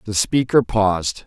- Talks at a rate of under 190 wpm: Yes, average, 140 wpm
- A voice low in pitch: Yes, low, 105 Hz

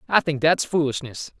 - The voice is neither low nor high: Yes, medium, 145 Hz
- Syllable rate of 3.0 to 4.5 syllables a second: No, 5.2 syllables/s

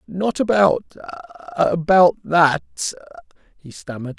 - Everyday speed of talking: No, slow, 70 wpm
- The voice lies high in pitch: No, medium, 150 Hz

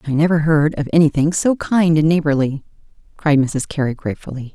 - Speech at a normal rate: Yes, average, 170 wpm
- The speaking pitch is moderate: Yes, medium, 155 Hz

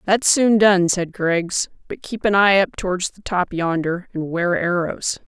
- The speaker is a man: No, female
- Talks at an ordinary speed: Yes, average, 190 wpm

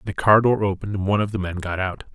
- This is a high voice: No, low, 100 Hz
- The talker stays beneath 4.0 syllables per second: No, 7.1 syllables/s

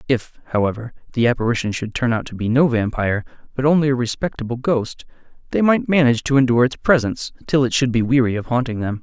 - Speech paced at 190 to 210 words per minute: Yes, fast, 205 wpm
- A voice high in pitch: No, low, 125 Hz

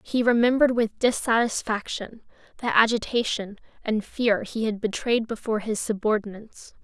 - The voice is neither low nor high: No, high, 225 Hz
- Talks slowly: Yes, slow, 125 wpm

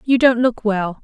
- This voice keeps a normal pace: No, fast, 230 wpm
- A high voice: Yes, high, 225 Hz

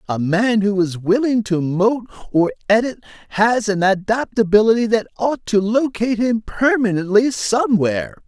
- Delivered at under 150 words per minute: Yes, average, 140 wpm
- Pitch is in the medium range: No, high, 215 Hz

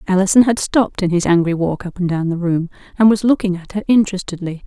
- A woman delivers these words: Yes, female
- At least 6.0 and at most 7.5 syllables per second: Yes, 6.5 syllables/s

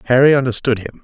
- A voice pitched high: No, low, 125 Hz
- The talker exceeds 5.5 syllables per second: Yes, 7.2 syllables/s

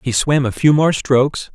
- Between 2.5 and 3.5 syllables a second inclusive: No, 4.8 syllables/s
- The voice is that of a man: Yes, male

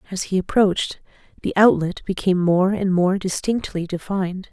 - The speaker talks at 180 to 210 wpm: No, average, 145 wpm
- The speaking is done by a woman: Yes, female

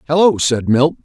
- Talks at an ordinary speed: Yes, average, 175 wpm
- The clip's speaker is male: Yes, male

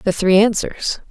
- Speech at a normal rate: Yes, average, 165 wpm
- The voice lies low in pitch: No, high, 200 Hz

